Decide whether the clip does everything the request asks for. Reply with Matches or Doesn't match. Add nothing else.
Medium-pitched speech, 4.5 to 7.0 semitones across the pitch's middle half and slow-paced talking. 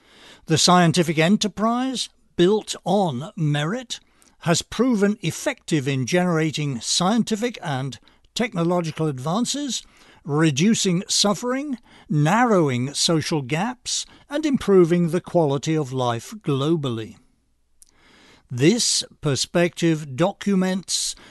Matches